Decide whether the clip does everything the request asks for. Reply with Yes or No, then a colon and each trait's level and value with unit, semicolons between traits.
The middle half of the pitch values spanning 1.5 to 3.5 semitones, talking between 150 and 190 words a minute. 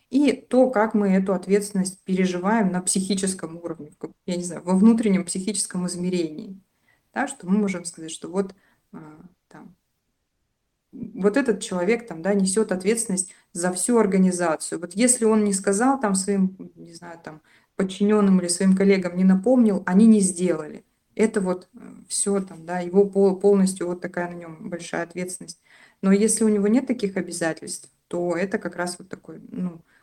Yes: average, 2.9 semitones; fast, 160 wpm